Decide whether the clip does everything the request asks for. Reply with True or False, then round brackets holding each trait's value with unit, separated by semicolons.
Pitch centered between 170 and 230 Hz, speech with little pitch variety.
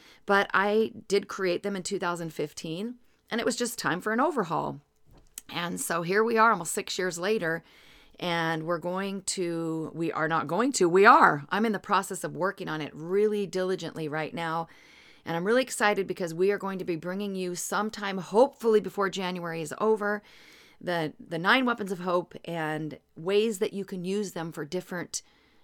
False (185 Hz; 3.8 semitones)